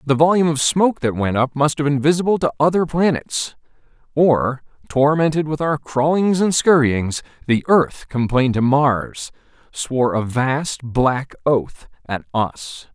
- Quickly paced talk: No, average, 150 wpm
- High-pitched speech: No, medium, 140 Hz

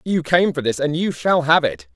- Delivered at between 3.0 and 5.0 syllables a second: Yes, 4.9 syllables/s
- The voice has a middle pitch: Yes, medium, 150 Hz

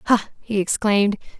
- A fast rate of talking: No, slow, 130 wpm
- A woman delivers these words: Yes, female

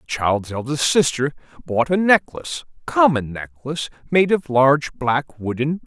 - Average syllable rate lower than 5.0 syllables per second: Yes, 4.6 syllables/s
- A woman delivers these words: No, male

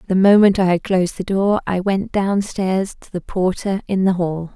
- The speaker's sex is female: Yes, female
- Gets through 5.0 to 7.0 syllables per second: No, 4.8 syllables/s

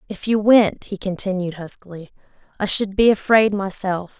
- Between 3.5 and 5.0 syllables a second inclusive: Yes, 4.8 syllables/s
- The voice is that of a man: No, female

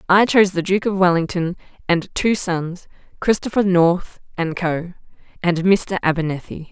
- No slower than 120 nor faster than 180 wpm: Yes, average, 145 wpm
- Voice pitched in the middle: Yes, medium, 180 Hz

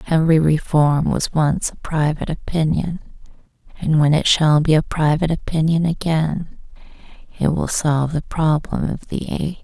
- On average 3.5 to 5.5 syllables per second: Yes, 4.9 syllables/s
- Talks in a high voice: No, medium, 155 Hz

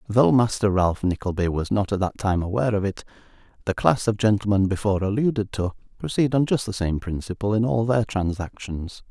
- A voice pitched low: Yes, low, 100 Hz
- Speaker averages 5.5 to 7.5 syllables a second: Yes, 5.6 syllables/s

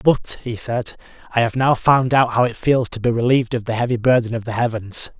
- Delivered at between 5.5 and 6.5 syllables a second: Yes, 5.6 syllables/s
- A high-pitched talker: No, low, 120 Hz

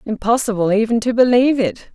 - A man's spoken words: No, female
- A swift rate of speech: No, average, 155 wpm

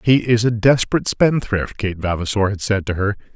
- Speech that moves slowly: No, average, 195 wpm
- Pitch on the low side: Yes, low, 110 Hz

